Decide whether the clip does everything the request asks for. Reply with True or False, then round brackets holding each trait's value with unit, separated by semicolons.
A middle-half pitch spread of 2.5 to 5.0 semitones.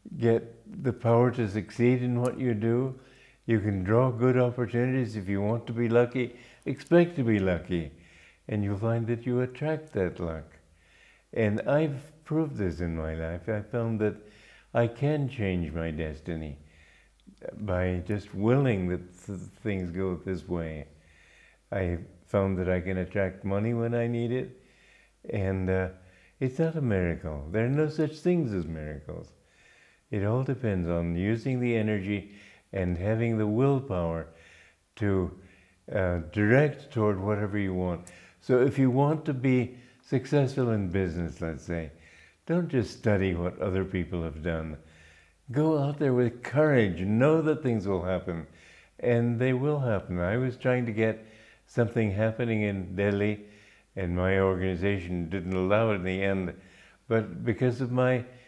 False (5.4 semitones)